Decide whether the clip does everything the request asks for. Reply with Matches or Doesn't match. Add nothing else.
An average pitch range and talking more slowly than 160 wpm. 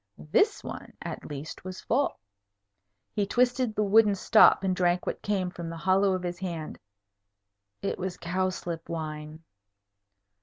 Matches